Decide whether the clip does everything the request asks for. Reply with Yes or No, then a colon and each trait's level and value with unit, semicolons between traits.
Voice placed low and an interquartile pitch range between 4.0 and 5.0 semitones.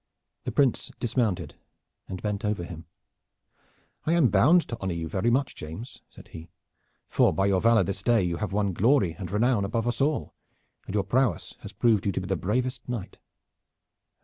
Yes: low, 105 Hz; average, 4.3 semitones